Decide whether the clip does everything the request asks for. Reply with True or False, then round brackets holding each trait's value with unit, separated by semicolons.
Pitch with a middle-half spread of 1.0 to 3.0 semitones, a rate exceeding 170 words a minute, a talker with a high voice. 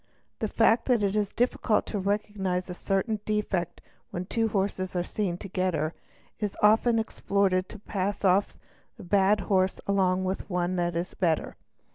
False (2.4 semitones; 160 wpm; 195 Hz)